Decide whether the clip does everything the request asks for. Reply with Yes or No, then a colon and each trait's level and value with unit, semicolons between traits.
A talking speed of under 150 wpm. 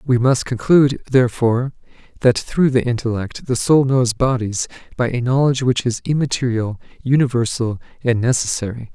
Yes: average, 140 wpm